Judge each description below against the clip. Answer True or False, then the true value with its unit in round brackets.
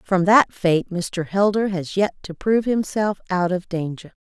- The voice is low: False (185 Hz)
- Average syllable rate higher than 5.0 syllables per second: False (4.5 syllables/s)